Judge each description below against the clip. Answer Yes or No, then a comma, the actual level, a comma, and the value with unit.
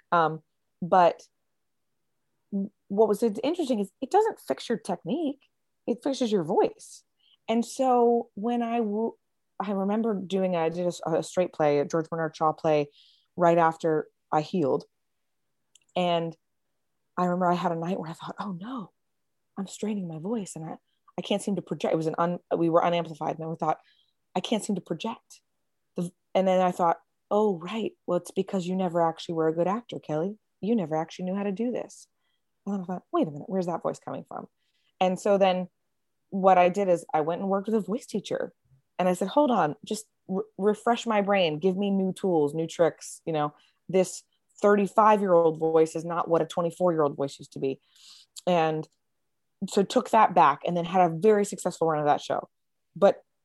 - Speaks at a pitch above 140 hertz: Yes, medium, 185 Hz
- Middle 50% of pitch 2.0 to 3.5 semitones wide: No, average, 4.2 semitones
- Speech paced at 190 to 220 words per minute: Yes, average, 200 wpm